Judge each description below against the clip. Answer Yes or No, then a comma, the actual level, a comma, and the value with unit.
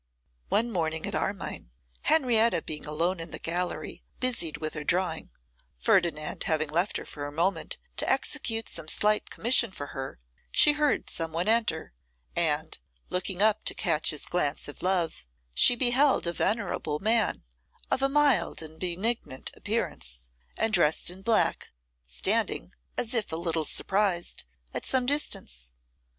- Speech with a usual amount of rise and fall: No, wide, 6.2 semitones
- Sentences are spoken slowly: No, average, 150 wpm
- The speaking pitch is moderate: Yes, medium, 175 Hz